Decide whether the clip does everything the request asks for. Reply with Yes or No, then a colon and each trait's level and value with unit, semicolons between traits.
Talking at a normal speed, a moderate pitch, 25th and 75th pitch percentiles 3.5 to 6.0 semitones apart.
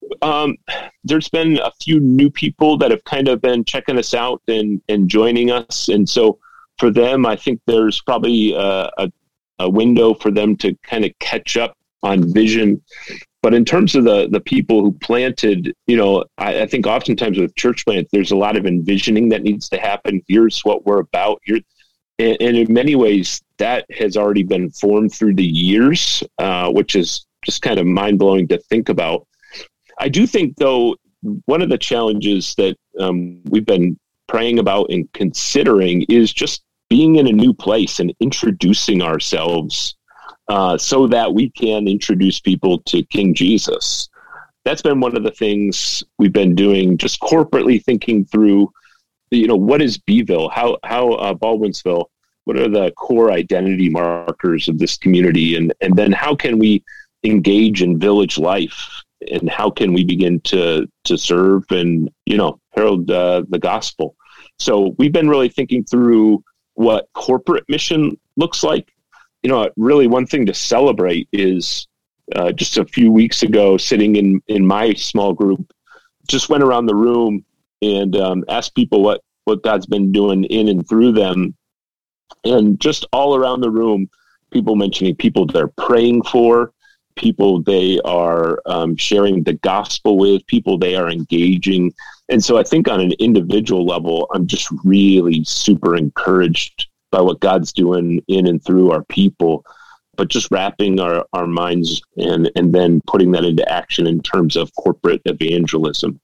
No: average, 170 wpm; low, 100 Hz; average, 4.3 semitones